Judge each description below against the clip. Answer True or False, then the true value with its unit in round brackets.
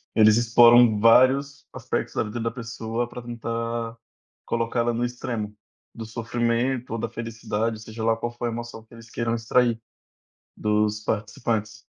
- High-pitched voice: False (115 Hz)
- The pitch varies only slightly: True (1.1 semitones)